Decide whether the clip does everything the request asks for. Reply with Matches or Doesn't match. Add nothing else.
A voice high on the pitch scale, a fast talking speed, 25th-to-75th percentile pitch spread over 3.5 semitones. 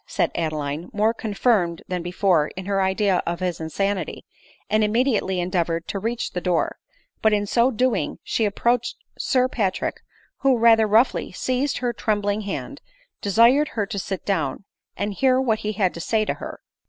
Doesn't match